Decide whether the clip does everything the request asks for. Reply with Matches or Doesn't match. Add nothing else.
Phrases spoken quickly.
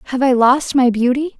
Matches